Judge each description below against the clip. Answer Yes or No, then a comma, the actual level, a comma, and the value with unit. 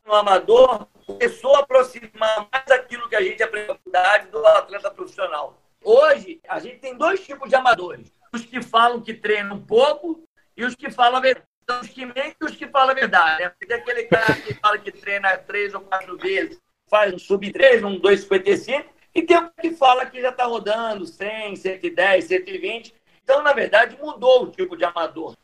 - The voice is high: Yes, very high, 255 Hz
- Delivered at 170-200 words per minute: Yes, fast, 185 wpm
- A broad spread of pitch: Yes, wide, 7.1 semitones